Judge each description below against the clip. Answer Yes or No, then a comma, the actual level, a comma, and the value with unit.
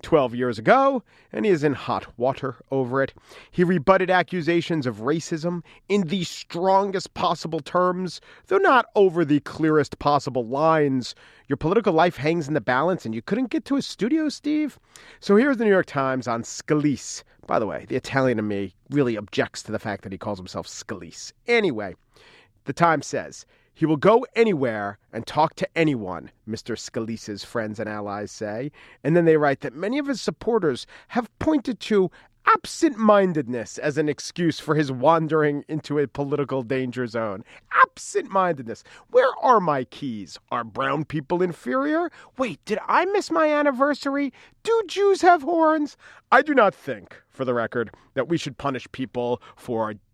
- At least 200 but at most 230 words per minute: No, average, 170 wpm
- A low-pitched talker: No, medium, 155 Hz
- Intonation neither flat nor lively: No, wide, 8.0 semitones